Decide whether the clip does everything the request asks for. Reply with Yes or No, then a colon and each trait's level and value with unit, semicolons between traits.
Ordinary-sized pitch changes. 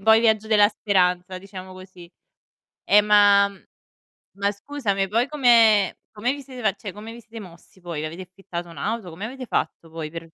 Yes: average, 3.3 semitones